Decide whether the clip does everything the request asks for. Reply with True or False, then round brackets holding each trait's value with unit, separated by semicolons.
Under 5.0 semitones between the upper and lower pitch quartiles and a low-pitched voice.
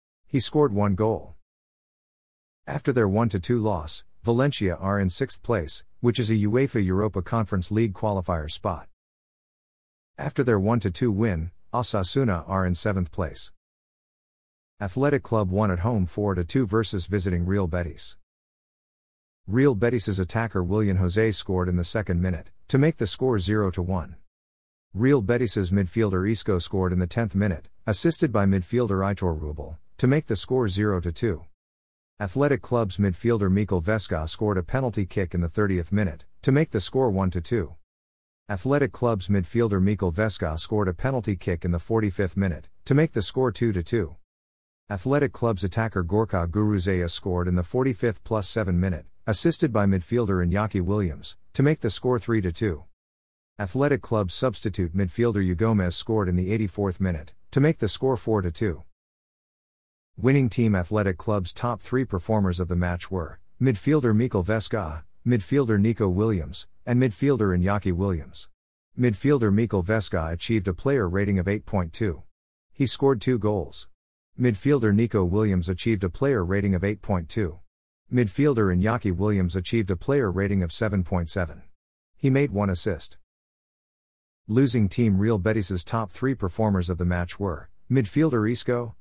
True (4.3 semitones; 100 Hz)